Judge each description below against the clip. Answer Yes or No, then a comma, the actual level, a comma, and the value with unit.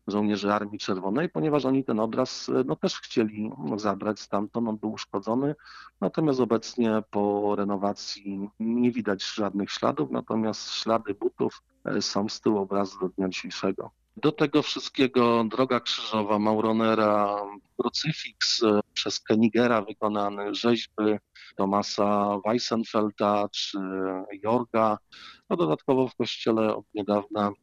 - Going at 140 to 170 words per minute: No, average, 120 wpm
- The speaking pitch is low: Yes, low, 110 Hz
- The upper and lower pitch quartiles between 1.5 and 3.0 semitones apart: Yes, narrow, 2.4 semitones